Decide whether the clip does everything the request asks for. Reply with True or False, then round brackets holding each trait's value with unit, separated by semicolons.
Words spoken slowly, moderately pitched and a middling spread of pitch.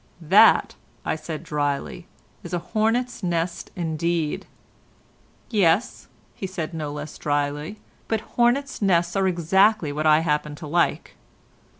True (125 wpm; 170 Hz; 4.5 semitones)